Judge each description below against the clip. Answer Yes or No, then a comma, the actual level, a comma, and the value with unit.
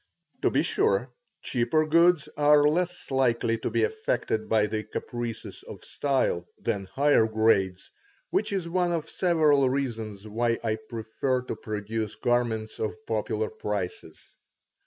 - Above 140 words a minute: No, slow, 135 wpm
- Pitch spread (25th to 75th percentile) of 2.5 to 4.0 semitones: No, average, 5.1 semitones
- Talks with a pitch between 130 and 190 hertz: No, low, 115 Hz